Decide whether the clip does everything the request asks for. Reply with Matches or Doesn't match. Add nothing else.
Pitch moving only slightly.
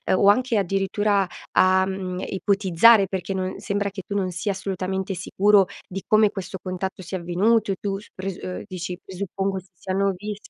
Matches